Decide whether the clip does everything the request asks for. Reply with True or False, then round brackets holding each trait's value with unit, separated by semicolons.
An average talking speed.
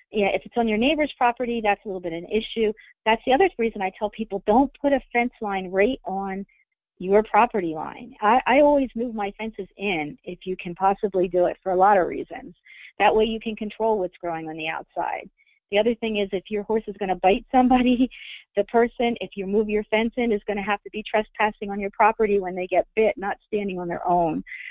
False (240 wpm)